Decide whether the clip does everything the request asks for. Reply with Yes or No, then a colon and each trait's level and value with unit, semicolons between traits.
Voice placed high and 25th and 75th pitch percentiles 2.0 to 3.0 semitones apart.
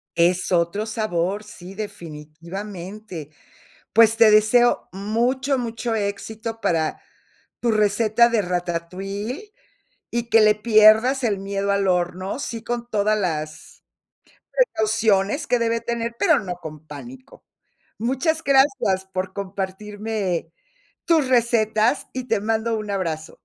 No: high, 215 Hz; average, 3.7 semitones